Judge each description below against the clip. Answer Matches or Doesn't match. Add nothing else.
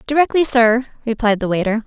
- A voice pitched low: Doesn't match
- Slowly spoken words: Doesn't match